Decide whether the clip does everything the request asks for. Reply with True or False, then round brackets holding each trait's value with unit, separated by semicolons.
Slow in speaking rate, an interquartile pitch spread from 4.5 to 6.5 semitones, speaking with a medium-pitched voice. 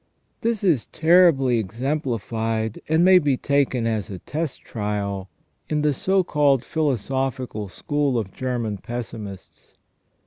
False (125 wpm; 5.2 semitones; 130 Hz)